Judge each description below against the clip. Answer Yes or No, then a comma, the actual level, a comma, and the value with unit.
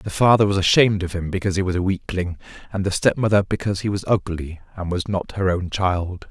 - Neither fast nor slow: No, fast, 230 wpm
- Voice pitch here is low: Yes, very low, 95 Hz